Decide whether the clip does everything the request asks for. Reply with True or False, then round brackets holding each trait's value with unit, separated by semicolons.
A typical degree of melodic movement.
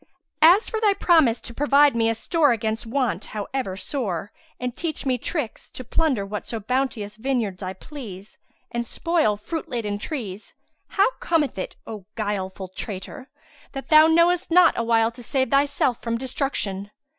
False (5.7 semitones)